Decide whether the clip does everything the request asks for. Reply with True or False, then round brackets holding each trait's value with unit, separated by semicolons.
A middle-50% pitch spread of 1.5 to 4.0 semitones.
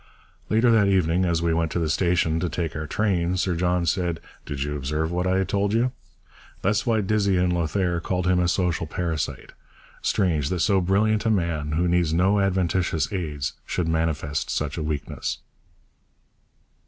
True (2.8 semitones)